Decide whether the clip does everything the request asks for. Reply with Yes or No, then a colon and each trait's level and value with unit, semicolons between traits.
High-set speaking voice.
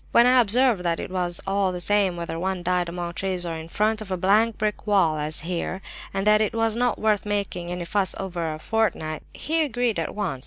Yes: high, 195 Hz